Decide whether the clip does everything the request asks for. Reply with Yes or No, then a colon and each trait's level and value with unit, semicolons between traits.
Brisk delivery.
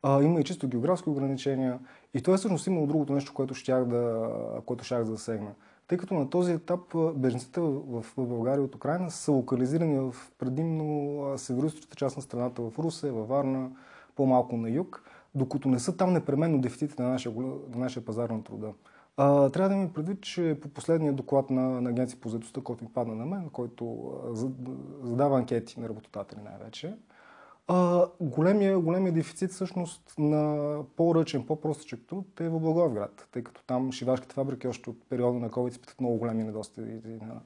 Yes: fast, 170 wpm